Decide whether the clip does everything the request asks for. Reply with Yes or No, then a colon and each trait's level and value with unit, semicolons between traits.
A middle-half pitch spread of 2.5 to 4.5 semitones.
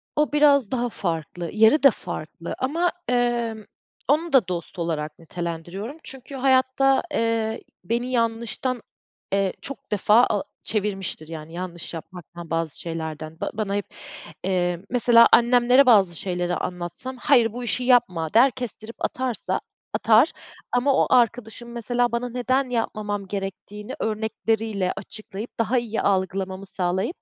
No: average, 5.2 semitones